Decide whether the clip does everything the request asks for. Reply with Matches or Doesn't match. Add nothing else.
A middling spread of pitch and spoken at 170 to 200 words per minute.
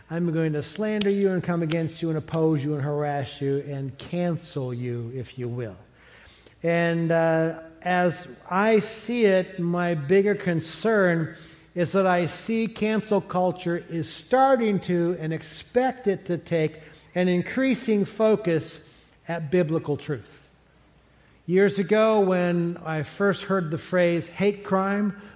Doesn't match